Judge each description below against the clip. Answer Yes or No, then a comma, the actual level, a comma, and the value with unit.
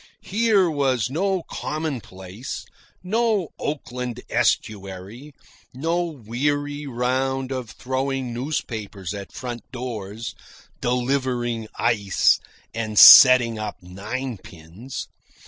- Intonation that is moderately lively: Yes, average, 4.6 semitones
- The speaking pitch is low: Yes, low, 125 Hz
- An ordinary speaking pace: No, slow, 85 wpm